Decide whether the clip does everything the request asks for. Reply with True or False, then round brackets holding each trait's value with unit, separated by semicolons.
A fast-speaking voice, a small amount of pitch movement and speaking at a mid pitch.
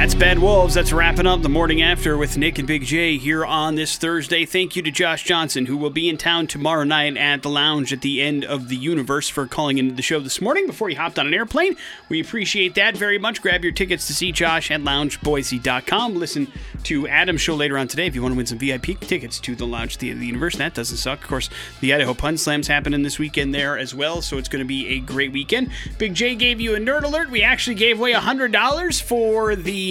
False (255 wpm; 5.1 semitones; 160 Hz)